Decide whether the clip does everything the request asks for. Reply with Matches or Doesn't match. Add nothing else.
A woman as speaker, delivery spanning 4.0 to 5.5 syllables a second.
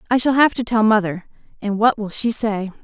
Matches